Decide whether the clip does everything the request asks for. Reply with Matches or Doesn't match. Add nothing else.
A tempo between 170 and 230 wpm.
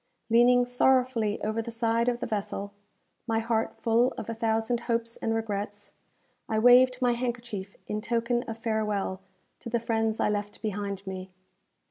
Doesn't match